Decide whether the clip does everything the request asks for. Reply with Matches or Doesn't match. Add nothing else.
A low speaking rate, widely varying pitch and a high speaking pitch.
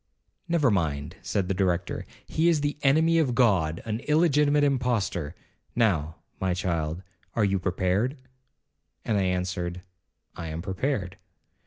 Doesn't match